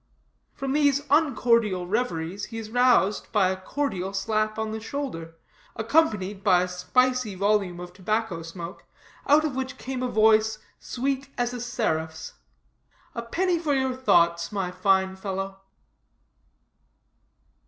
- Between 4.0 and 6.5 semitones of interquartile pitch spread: Yes, average, 5.2 semitones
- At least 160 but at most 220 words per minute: No, slow, 135 wpm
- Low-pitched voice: No, high, 215 Hz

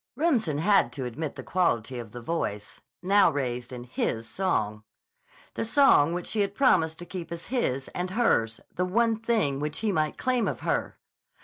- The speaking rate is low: No, average, 185 wpm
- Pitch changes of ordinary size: No, wide, 8.6 semitones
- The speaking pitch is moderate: Yes, medium, 165 Hz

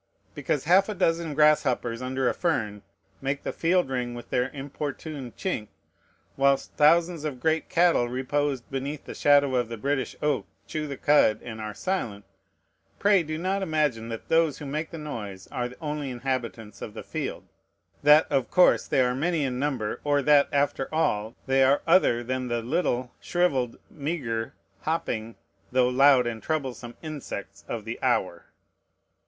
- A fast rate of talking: No, average, 165 wpm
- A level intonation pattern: No, average, 4.2 semitones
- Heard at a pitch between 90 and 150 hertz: Yes, low, 135 Hz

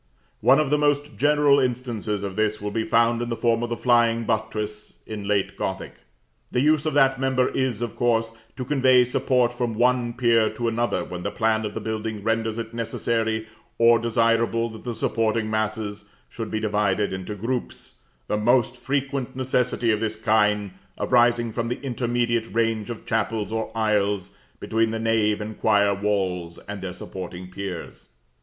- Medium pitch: No, low, 115 Hz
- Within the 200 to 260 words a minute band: No, average, 175 wpm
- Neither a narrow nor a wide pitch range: No, narrow, 2.3 semitones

